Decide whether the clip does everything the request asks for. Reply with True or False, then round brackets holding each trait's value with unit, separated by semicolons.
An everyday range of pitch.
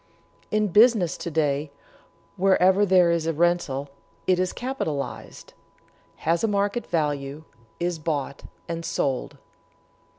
True (4.3 semitones)